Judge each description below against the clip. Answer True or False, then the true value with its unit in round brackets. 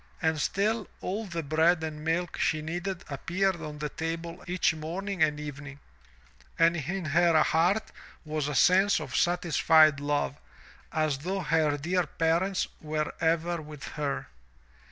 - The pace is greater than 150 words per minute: False (145 wpm)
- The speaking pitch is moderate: True (160 Hz)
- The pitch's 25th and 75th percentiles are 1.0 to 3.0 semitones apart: True (2.7 semitones)